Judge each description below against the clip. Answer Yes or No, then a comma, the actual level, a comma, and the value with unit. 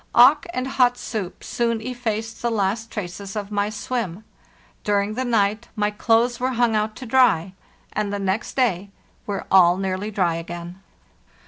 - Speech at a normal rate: Yes, average, 160 wpm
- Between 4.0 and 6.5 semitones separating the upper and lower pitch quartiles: No, average, 3.4 semitones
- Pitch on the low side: No, high, 215 Hz